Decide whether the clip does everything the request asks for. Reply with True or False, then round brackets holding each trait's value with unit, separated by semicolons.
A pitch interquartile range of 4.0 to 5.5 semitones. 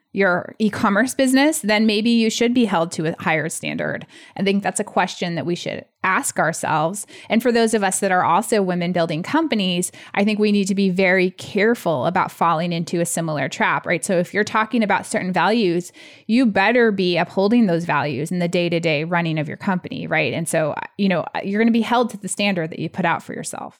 True (4.3 semitones)